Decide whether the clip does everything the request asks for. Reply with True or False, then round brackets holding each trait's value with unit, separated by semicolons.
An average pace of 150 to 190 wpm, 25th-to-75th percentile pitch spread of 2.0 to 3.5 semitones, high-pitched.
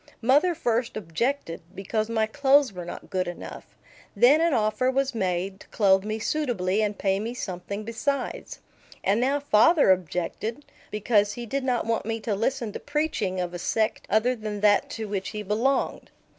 False (175 wpm; 4.6 semitones; 220 Hz)